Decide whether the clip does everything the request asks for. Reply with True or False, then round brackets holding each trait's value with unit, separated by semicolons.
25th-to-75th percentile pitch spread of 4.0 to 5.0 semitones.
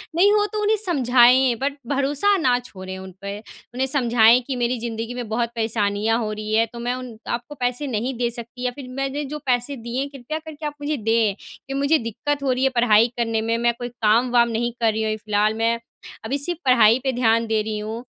False (3.1 semitones)